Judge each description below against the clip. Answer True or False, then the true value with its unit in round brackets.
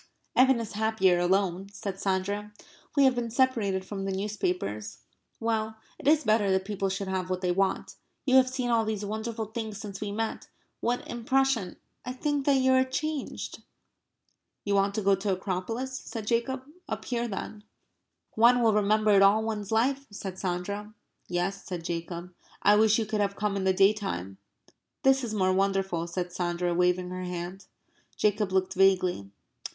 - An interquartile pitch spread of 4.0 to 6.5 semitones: False (3.4 semitones)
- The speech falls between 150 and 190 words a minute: True (175 wpm)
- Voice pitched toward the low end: False (205 Hz)